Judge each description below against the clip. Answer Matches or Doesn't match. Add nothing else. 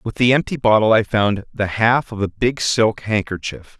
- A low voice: Matches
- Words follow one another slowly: Doesn't match